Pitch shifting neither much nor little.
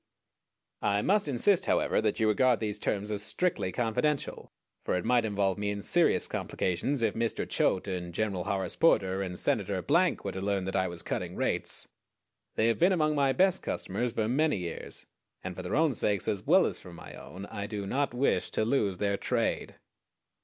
Yes: average, 5.0 semitones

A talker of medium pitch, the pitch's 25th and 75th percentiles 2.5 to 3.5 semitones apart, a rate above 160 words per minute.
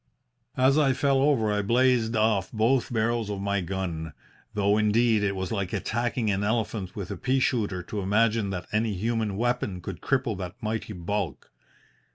No: low, 110 Hz; average, 3.2 semitones; average, 175 wpm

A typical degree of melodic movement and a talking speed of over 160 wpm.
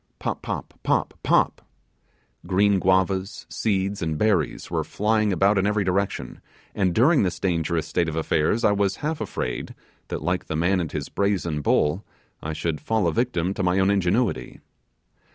Yes: average, 3.2 semitones; average, 170 wpm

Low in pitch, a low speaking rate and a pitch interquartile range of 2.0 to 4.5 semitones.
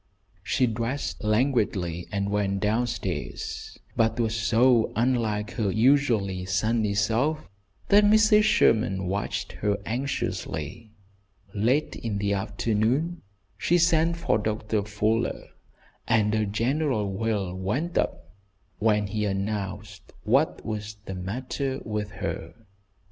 Yes: low, 110 Hz; slow, 115 wpm; average, 3.6 semitones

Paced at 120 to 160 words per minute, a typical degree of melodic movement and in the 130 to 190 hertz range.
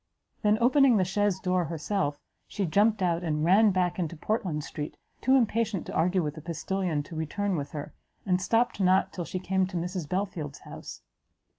No: average, 185 wpm; average, 3.9 semitones; medium, 185 Hz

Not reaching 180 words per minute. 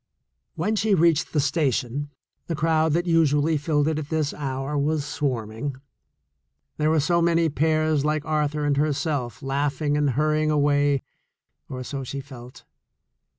Yes: average, 150 wpm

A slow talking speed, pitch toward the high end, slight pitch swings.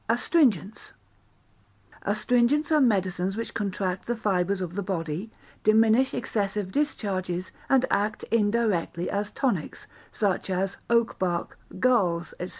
No: slow, 120 wpm; high, 205 Hz; average, 4.0 semitones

